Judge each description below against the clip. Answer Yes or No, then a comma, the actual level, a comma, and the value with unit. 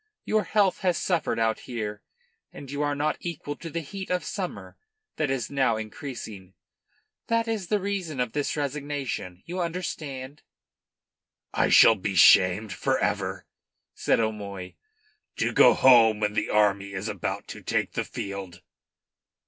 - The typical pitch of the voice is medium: No, low, 130 Hz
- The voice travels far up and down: Yes, wide, 7.6 semitones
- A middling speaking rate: Yes, average, 150 wpm